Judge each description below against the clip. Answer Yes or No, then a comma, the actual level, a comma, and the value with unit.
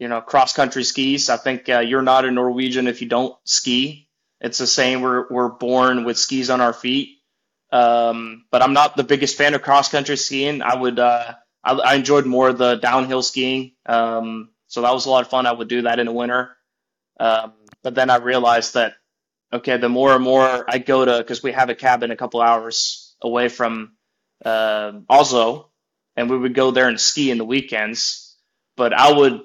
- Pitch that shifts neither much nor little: No, narrow, 1.7 semitones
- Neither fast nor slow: No, fast, 210 wpm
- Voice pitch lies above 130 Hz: No, low, 125 Hz